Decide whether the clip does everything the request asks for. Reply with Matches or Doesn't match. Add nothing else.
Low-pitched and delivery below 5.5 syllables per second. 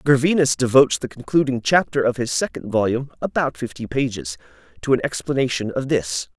Doesn't match